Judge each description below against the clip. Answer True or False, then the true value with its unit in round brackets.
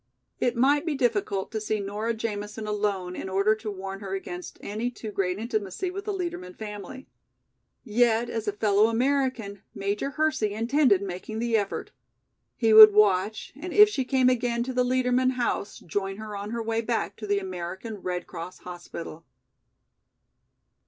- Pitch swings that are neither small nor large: True (3.7 semitones)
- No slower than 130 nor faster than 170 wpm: True (165 wpm)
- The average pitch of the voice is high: True (215 Hz)